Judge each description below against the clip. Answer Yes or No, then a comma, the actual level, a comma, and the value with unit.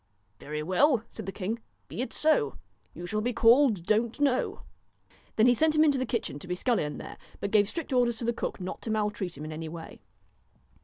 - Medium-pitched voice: No, high, 220 Hz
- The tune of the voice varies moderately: No, wide, 5.7 semitones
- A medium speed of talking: No, fast, 225 wpm